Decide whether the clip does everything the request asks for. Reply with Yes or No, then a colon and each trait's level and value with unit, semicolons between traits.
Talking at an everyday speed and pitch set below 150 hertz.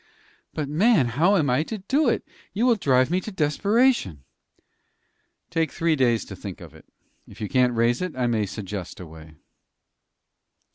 Yes: average, 175 wpm; low, 135 Hz